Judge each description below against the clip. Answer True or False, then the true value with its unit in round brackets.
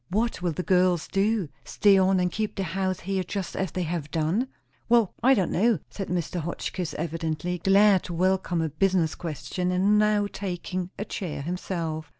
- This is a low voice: False (185 Hz)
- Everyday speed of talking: True (180 wpm)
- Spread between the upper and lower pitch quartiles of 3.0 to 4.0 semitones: False (2.5 semitones)